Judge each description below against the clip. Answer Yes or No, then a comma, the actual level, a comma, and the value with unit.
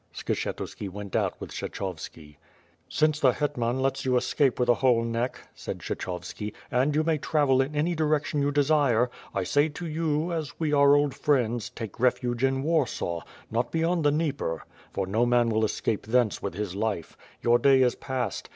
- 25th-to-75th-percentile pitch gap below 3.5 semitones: No, average, 4.4 semitones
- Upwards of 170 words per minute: Yes, average, 180 wpm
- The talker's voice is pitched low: Yes, low, 130 Hz